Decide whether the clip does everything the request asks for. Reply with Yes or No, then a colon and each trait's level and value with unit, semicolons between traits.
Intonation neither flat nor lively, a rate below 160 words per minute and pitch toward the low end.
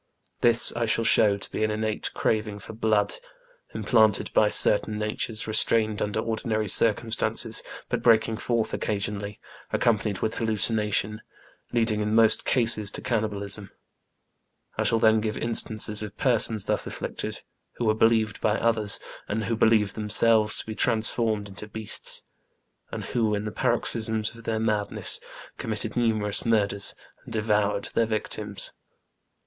No: narrow, 1.2 semitones; average, 150 wpm; low, 110 Hz